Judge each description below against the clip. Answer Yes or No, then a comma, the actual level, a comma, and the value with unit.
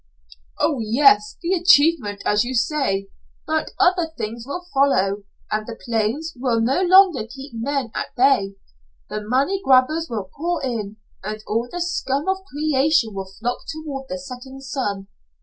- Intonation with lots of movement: Yes, wide, 5.9 semitones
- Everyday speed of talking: Yes, average, 155 wpm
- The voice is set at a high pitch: Yes, very high, 265 Hz